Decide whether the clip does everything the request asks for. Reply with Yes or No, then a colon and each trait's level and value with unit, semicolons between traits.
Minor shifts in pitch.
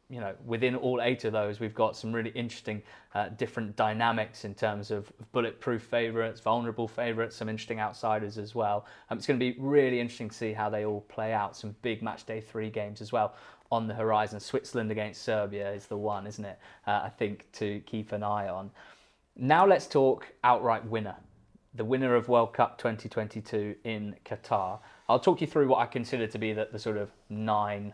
Yes: narrow, 2.0 semitones